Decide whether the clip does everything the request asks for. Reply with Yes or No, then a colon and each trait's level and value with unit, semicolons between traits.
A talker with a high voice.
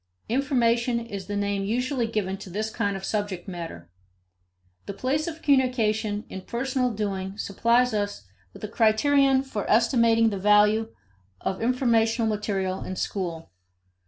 Yes: high, 220 Hz